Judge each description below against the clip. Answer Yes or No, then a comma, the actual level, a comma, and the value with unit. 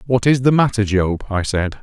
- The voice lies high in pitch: No, low, 110 Hz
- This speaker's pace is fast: Yes, fast, 230 wpm